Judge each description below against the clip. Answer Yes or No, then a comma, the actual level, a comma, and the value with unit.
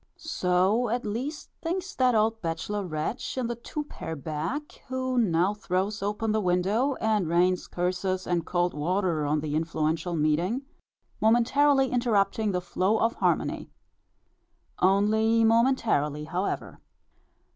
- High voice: Yes, high, 205 Hz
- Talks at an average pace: No, slow, 130 wpm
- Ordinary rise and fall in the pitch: Yes, average, 4.9 semitones